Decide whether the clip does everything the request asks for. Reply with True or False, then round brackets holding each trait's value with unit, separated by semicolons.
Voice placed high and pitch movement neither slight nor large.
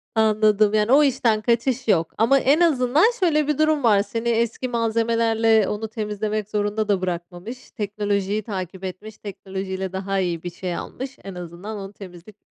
True (215 Hz; 3.2 semitones)